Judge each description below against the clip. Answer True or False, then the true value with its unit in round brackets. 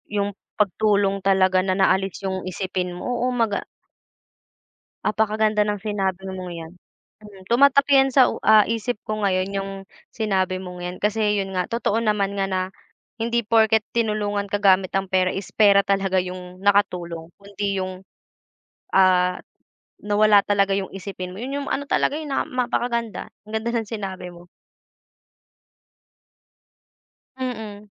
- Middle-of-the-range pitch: False (200 Hz)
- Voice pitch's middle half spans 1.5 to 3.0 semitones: True (2.6 semitones)